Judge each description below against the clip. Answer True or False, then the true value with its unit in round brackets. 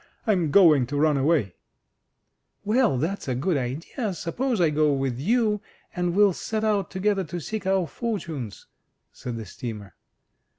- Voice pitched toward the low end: False (170 Hz)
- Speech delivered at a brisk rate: False (160 wpm)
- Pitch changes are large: True (7.1 semitones)